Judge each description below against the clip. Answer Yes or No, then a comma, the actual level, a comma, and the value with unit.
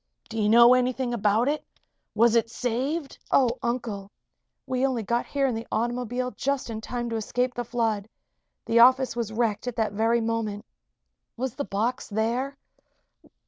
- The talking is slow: No, average, 165 wpm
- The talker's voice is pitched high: Yes, high, 235 Hz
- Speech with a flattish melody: Yes, narrow, 2.2 semitones